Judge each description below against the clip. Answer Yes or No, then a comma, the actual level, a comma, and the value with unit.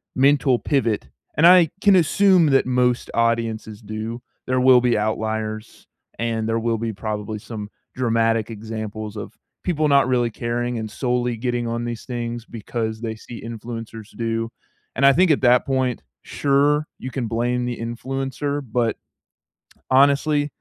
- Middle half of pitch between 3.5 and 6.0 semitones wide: No, average, 2.8 semitones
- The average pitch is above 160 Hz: No, low, 120 Hz